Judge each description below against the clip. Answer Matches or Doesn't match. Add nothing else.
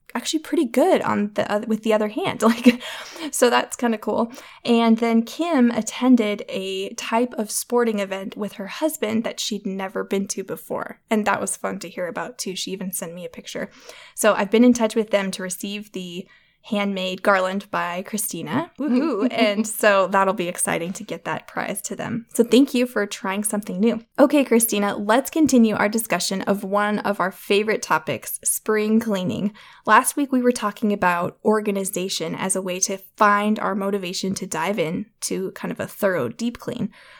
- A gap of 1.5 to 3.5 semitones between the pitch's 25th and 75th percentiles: Matches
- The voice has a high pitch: Matches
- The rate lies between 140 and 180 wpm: Doesn't match